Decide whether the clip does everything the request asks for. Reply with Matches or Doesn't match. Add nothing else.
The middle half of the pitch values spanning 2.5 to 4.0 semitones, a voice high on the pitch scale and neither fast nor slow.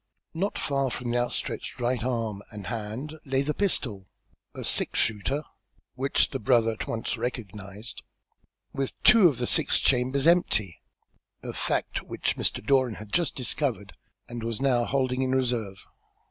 Doesn't match